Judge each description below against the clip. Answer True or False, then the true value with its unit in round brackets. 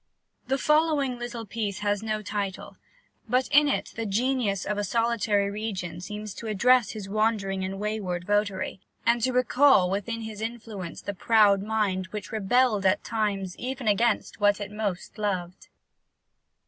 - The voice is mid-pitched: False (210 Hz)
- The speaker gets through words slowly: False (155 wpm)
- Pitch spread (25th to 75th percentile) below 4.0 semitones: True (2.9 semitones)